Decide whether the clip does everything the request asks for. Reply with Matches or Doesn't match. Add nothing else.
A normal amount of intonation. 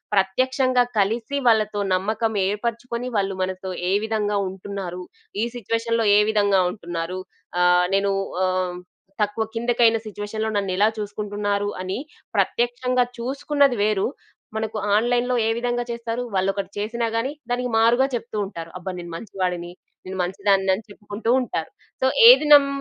Matches